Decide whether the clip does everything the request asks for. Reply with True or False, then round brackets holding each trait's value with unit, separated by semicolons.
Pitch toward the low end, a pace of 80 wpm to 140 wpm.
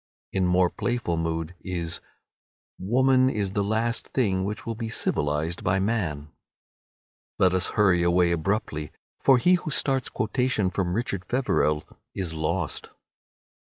True (95 Hz; 135 wpm)